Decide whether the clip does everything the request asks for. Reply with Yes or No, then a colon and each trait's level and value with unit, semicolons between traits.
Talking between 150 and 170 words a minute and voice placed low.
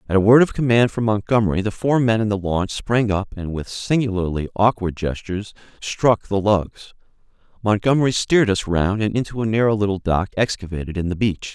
No: average, 190 wpm; low, 105 Hz